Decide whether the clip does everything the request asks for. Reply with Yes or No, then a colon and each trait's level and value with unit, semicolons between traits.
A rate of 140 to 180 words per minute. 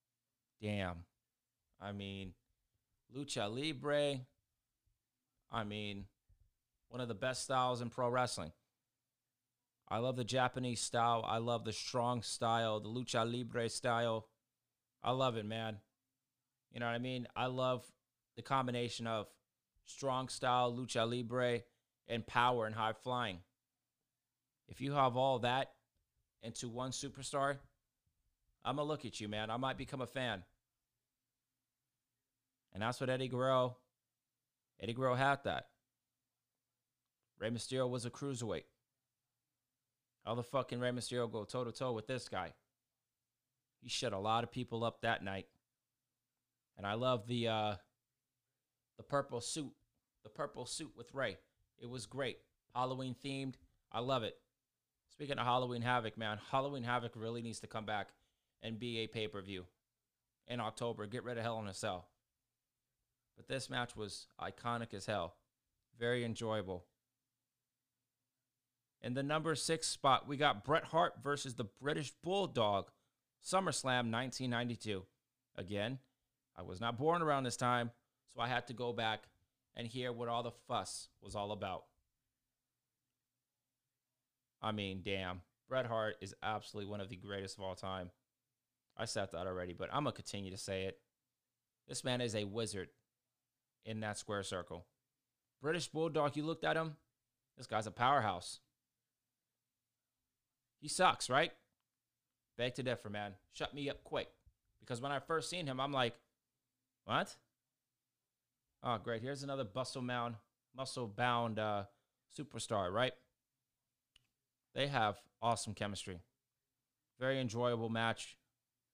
Yes: average, 145 wpm